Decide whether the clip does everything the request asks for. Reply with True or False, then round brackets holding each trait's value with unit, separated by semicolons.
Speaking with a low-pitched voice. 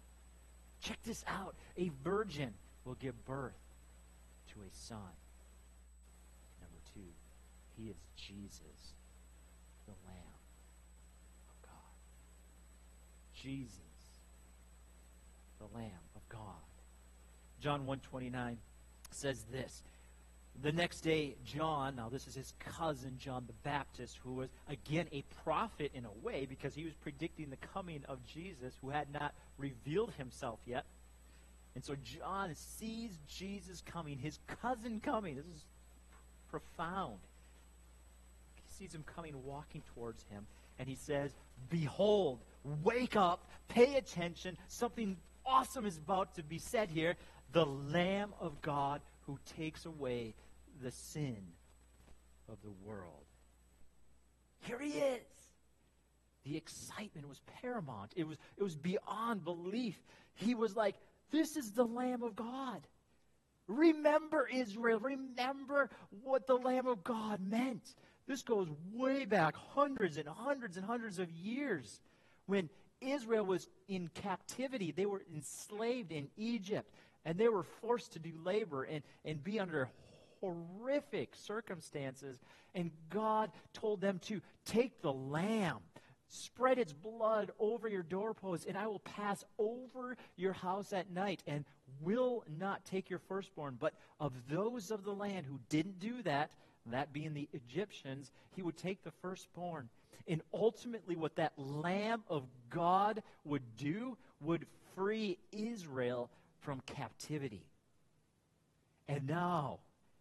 False (155 Hz)